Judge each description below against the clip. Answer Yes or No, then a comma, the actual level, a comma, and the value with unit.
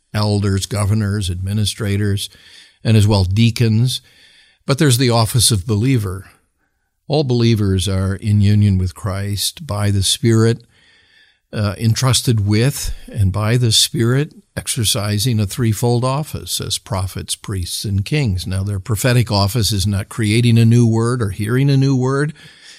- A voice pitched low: Yes, low, 110 Hz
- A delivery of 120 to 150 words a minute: Yes, average, 140 wpm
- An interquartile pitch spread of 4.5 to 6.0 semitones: No, average, 3.4 semitones